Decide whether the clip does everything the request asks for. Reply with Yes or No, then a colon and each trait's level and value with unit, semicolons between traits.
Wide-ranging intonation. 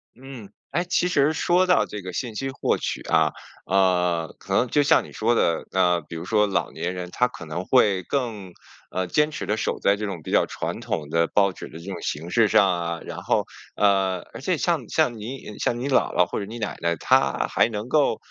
Yes: wide, 5.7 semitones